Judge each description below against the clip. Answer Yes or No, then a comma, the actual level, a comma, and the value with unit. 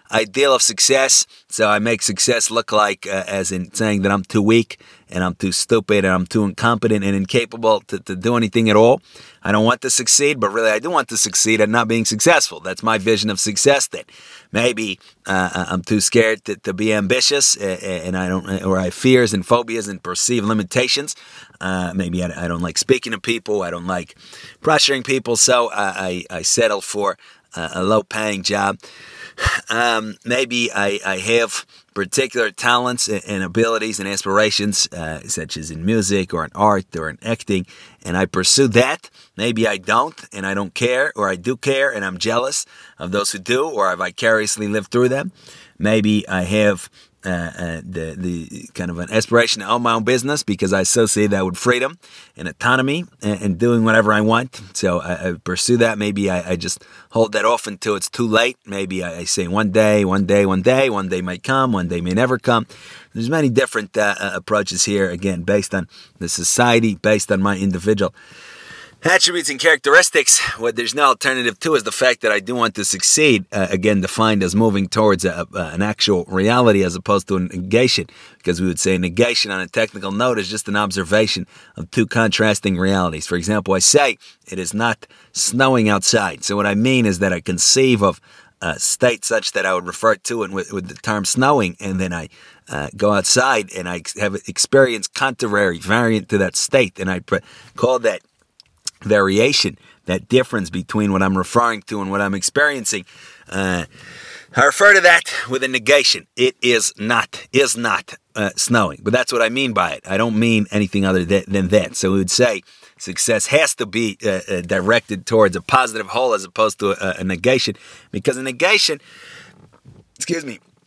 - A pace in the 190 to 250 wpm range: Yes, average, 200 wpm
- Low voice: Yes, low, 105 Hz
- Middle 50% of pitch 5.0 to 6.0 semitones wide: No, average, 3.6 semitones